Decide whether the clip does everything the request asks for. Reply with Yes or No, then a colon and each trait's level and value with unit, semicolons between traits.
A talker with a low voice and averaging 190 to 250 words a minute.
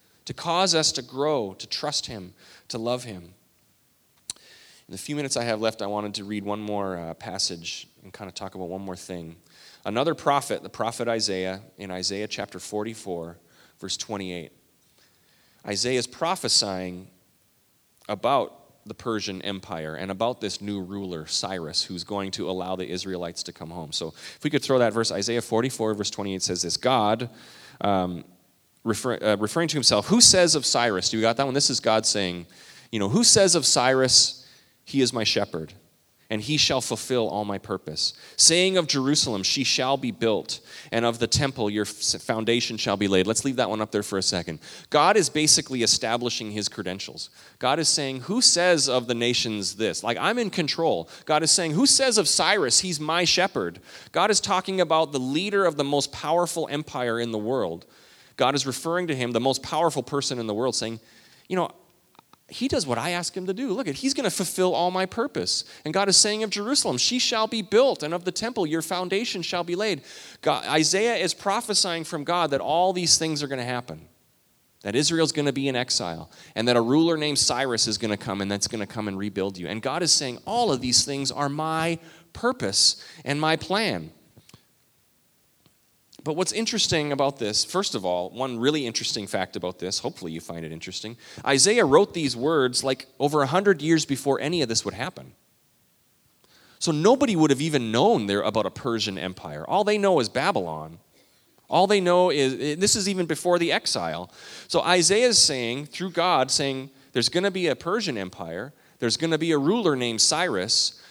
Yes: low, 125 Hz; average, 200 wpm